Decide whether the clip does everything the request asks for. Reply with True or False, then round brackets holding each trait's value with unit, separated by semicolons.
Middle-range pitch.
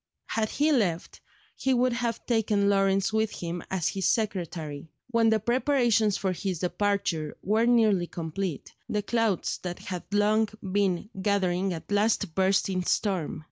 False (200 Hz)